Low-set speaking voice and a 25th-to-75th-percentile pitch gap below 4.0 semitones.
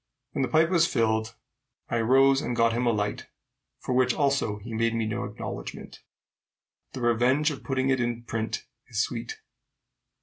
Yes: low, 120 Hz; average, 2.9 semitones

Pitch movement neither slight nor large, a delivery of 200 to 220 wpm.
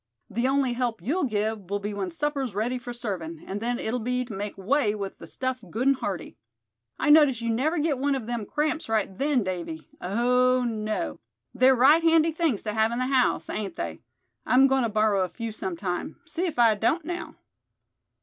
Yes: average, 4.5 semitones; fast, 205 wpm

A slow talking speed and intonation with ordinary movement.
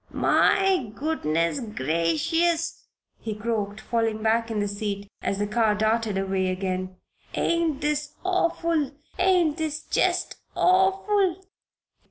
No: slow, 115 wpm; wide, 8.6 semitones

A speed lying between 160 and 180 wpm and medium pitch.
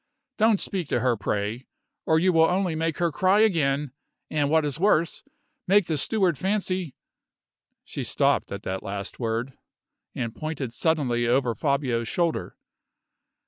No: average, 150 wpm; medium, 155 Hz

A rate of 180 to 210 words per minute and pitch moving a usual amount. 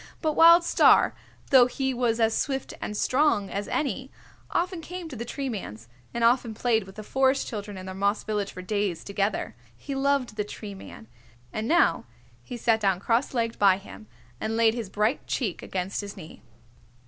Yes: average, 190 wpm; average, 4.7 semitones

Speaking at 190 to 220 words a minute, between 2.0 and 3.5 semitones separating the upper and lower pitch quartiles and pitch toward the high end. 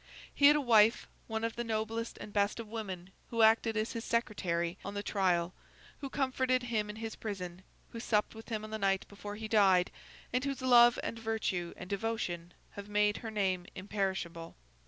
Yes: average, 195 wpm; average, 3.0 semitones; high, 215 Hz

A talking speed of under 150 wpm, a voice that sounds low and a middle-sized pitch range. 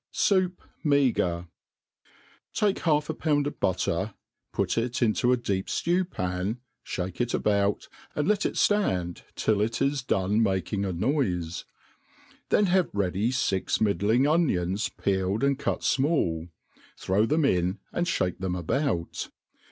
No: average, 140 wpm; low, 110 Hz; wide, 7.8 semitones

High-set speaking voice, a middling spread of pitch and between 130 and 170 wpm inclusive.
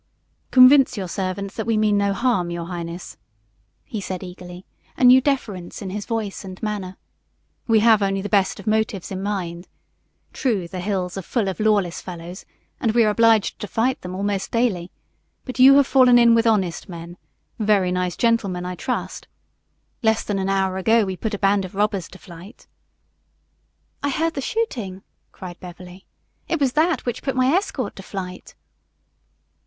No: high, 200 Hz; average, 3.9 semitones; average, 180 wpm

